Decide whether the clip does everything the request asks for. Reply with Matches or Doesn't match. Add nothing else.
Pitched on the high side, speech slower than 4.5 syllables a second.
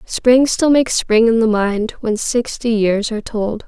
Matches